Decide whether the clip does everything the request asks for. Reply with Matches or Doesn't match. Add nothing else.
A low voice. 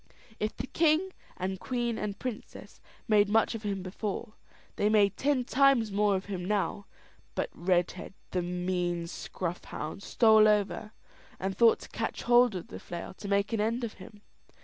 Doesn't match